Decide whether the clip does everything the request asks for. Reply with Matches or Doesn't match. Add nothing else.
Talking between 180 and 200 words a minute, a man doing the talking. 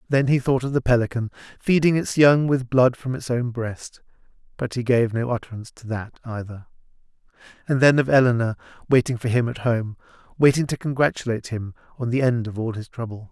Matches